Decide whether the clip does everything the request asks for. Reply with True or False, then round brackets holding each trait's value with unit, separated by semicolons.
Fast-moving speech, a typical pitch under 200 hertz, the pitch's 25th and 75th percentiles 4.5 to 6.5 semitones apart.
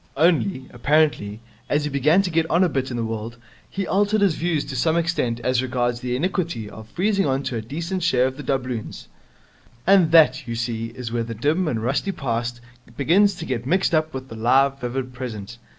True (210 wpm; 135 Hz; 5.6 semitones)